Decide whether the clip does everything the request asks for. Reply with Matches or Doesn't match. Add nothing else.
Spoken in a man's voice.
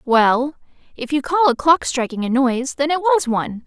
Doesn't match